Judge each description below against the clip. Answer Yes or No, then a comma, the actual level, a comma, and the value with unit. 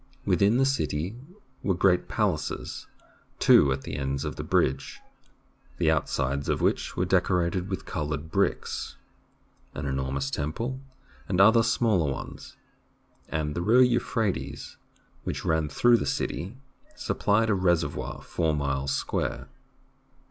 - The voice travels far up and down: Yes, wide, 6.6 semitones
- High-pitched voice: No, very low, 85 Hz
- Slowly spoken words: Yes, slow, 130 wpm